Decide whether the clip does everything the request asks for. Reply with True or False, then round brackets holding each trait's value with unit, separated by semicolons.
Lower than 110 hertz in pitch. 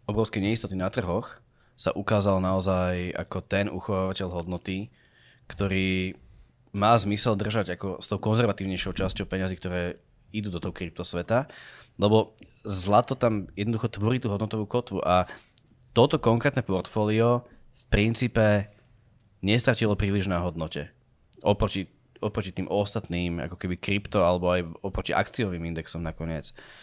True (100 Hz)